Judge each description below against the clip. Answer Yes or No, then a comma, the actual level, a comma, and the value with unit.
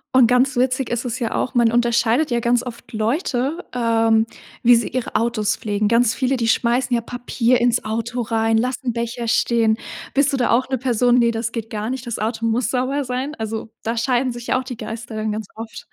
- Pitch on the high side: Yes, high, 235 Hz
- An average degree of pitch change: No, narrow, 1.9 semitones